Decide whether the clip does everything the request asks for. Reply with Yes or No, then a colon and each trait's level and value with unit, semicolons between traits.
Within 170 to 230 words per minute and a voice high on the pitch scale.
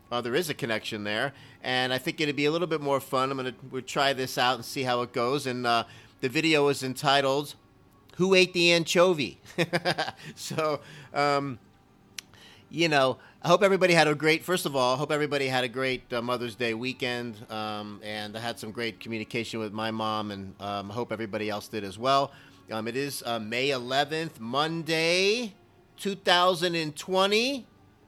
No: average, 190 wpm; low, 130 Hz